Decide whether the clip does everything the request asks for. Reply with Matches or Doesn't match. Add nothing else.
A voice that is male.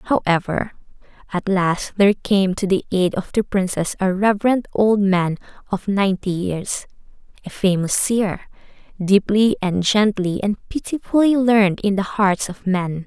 Doesn't match